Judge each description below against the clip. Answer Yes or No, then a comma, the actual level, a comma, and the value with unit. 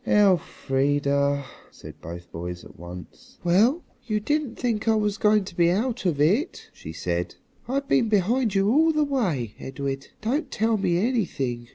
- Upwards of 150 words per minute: Yes, average, 165 wpm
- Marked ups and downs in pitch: Yes, wide, 8.9 semitones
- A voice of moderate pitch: No, high, 195 Hz